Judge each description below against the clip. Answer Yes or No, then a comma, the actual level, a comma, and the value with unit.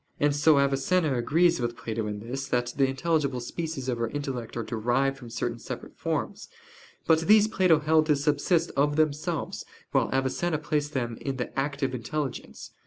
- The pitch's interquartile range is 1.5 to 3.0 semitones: No, average, 3.8 semitones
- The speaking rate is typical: Yes, average, 175 wpm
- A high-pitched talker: No, medium, 140 Hz